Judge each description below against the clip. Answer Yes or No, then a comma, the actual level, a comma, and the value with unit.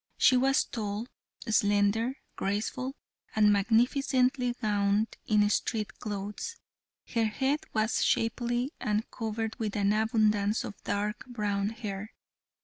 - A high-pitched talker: Yes, high, 215 Hz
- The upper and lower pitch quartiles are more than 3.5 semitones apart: No, average, 2.7 semitones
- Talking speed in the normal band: No, slow, 115 wpm